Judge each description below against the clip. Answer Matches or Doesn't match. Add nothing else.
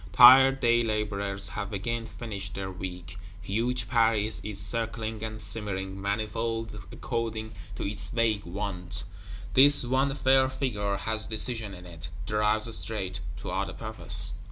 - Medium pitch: Doesn't match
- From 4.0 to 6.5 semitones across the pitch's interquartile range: Doesn't match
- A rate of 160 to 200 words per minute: Doesn't match